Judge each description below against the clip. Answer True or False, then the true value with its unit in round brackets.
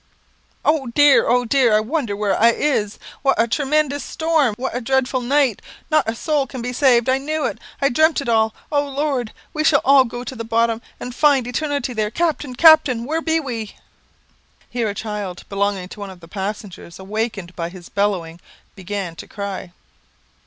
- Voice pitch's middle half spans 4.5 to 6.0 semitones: True (5.2 semitones)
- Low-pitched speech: False (240 Hz)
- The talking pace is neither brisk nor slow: True (195 wpm)